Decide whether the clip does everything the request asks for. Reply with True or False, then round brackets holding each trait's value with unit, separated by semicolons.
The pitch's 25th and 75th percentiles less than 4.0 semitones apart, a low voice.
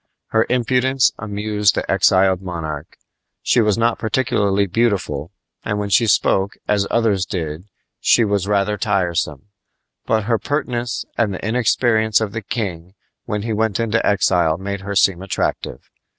True (2.9 semitones; 105 Hz)